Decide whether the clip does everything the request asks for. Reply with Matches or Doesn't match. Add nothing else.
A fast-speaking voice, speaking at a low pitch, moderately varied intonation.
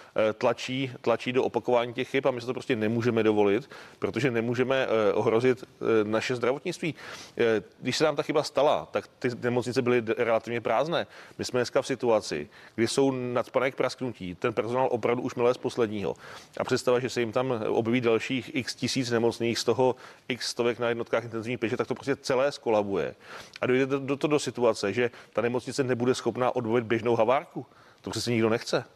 Doesn't match